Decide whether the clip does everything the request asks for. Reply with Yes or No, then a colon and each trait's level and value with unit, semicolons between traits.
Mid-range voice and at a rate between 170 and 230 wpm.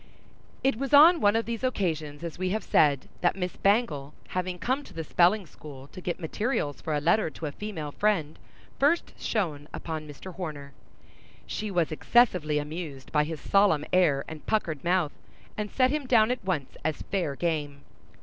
Yes: medium, 175 Hz; average, 180 wpm